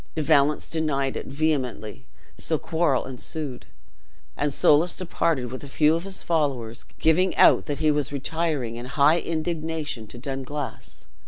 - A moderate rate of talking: Yes, average, 150 wpm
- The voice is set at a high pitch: No, medium, 145 Hz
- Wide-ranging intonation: No, average, 3.2 semitones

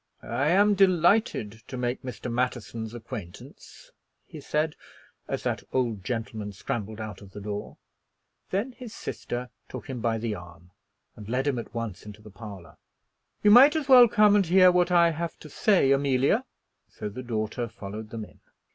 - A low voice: Yes, low, 120 Hz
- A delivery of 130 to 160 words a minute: No, average, 175 wpm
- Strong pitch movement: Yes, wide, 8.3 semitones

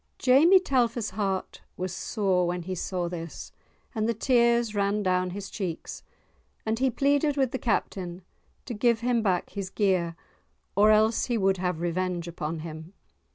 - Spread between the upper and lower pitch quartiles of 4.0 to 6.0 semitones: Yes, average, 4.7 semitones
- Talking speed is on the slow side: No, average, 160 wpm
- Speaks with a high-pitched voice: Yes, high, 200 Hz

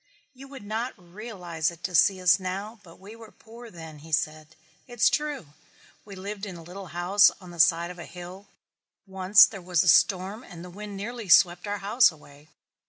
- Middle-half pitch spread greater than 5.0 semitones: No, average, 3.4 semitones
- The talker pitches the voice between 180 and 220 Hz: Yes, high, 190 Hz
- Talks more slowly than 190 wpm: No, average, 200 wpm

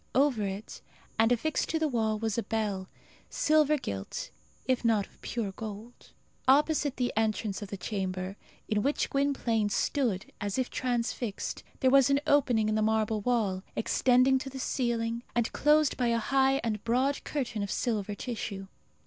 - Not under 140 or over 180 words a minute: Yes, average, 165 wpm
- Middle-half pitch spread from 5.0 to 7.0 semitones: No, average, 3.9 semitones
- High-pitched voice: Yes, high, 230 Hz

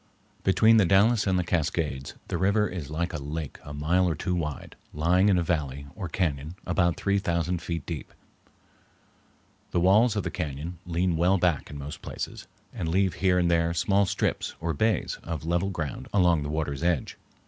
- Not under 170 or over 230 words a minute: Yes, average, 190 wpm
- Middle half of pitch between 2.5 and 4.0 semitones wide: Yes, average, 3.2 semitones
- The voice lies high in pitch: No, very low, 85 Hz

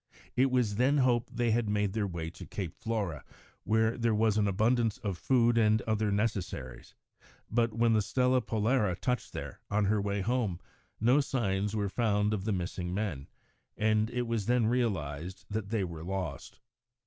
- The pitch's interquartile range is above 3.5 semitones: No, average, 3.1 semitones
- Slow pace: No, average, 180 wpm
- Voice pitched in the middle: No, low, 110 Hz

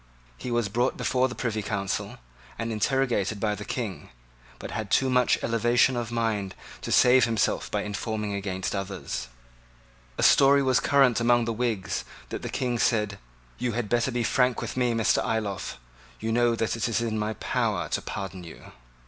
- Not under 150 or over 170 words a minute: No, average, 180 wpm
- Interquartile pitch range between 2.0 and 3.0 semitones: Yes, average, 2.7 semitones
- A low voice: Yes, low, 115 Hz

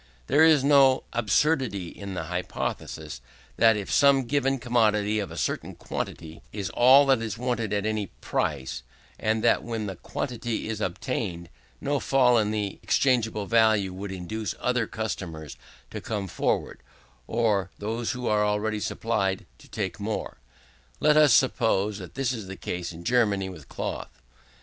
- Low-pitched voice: Yes, low, 110 Hz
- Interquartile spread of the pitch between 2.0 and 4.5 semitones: Yes, average, 4.2 semitones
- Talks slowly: No, average, 155 wpm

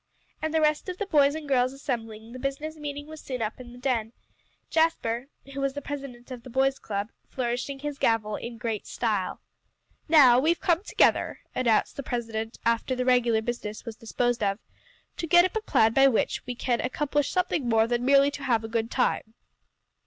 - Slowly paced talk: No, average, 195 wpm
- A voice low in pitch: No, very high, 255 Hz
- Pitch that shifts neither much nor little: Yes, average, 3.8 semitones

